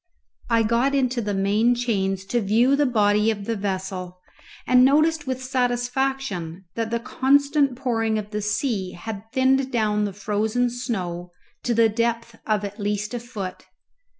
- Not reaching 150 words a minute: No, average, 160 wpm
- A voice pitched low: No, high, 225 Hz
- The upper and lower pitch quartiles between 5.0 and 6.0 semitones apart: No, average, 3.6 semitones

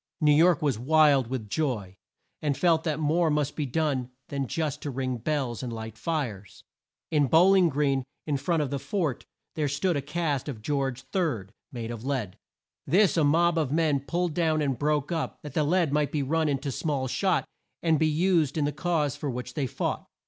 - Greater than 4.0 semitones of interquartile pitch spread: No, average, 3.3 semitones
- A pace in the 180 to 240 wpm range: Yes, fast, 205 wpm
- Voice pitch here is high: No, medium, 145 Hz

